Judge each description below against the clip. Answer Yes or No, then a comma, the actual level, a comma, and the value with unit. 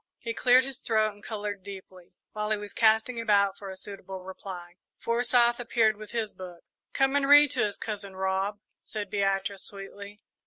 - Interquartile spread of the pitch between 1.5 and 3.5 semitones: Yes, average, 2.9 semitones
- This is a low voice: No, high, 205 Hz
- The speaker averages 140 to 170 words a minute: No, average, 180 wpm